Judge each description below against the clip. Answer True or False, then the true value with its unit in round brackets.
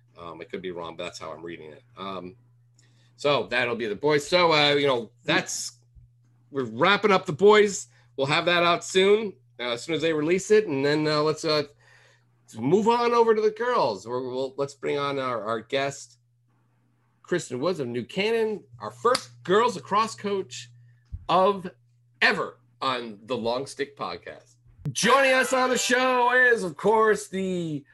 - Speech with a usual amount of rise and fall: False (7.9 semitones)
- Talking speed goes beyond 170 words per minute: True (185 wpm)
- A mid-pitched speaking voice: True (145 Hz)